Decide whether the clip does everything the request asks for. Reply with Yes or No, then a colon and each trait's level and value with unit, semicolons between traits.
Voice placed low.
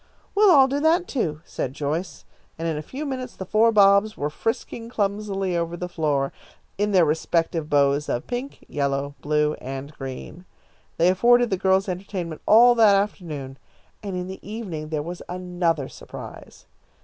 No: medium, 180 Hz